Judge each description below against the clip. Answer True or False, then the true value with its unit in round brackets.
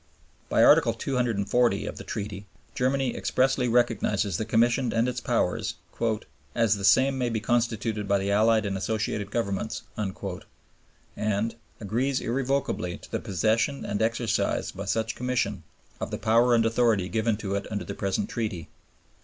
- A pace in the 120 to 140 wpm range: False (155 wpm)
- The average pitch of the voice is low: True (115 Hz)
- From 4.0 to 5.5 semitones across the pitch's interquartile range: False (3.1 semitones)